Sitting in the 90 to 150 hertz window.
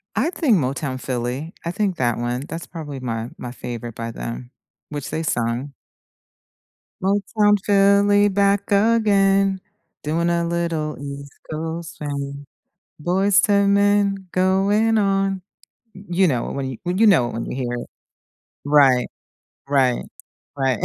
No: medium, 170 Hz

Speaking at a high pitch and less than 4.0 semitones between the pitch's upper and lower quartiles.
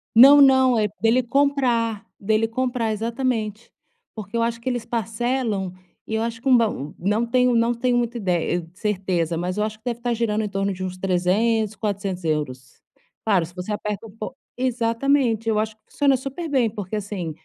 Yes: high, 225 Hz; average, 3.3 semitones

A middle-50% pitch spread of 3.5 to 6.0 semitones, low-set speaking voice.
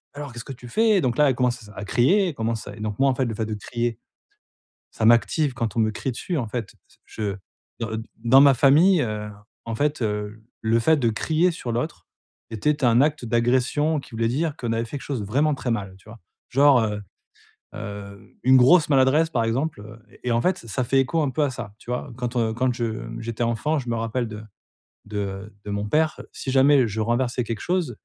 Yes: average, 3.8 semitones; low, 120 Hz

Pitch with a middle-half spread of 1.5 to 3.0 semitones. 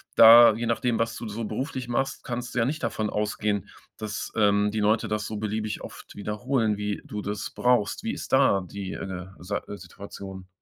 Yes: narrow, 2.5 semitones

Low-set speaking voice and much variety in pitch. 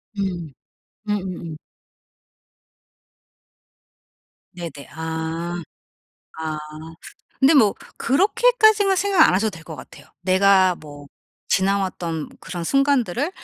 No: medium, 185 Hz; wide, 8.5 semitones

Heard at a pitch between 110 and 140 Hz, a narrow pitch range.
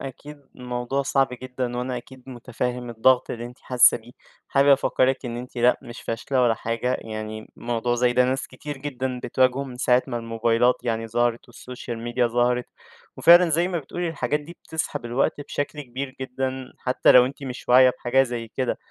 Yes: low, 125 Hz; narrow, 1.8 semitones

